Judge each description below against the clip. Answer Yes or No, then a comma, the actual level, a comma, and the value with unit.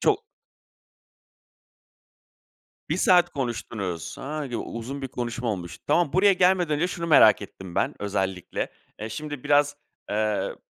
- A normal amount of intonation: No, wide, 6.7 semitones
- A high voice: No, low, 135 Hz